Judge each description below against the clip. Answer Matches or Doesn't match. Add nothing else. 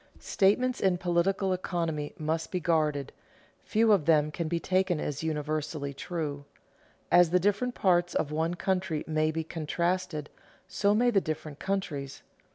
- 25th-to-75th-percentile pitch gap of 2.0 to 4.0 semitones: Matches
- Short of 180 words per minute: Matches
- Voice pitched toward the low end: Doesn't match